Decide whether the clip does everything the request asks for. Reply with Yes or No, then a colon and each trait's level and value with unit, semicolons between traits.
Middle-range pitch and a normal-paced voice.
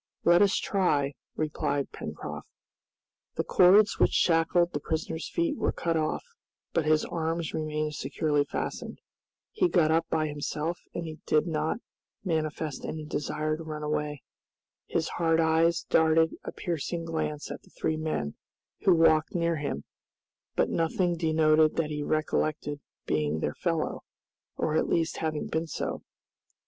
Yes: medium, 160 Hz; average, 145 wpm